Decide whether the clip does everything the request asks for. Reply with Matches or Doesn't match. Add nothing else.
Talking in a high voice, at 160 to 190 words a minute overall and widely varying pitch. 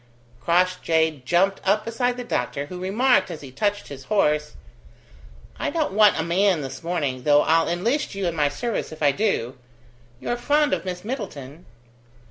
Doesn't match